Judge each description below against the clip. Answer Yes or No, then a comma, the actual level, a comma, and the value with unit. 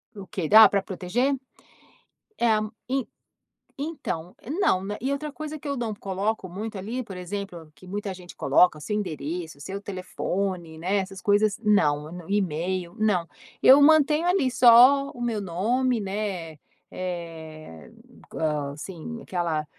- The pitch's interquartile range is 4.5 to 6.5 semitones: Yes, average, 5.2 semitones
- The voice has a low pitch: No, high, 195 Hz